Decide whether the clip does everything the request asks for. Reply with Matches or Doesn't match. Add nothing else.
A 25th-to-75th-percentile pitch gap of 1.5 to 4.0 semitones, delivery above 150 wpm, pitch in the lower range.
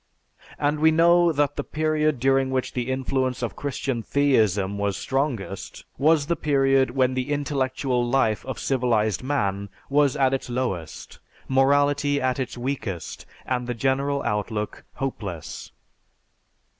Doesn't match